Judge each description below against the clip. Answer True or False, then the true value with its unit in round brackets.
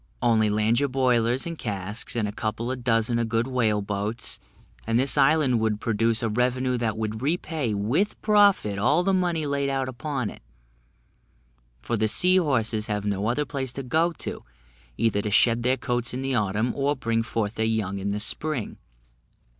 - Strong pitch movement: False (3.9 semitones)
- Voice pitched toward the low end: True (120 Hz)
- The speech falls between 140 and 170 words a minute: False (185 wpm)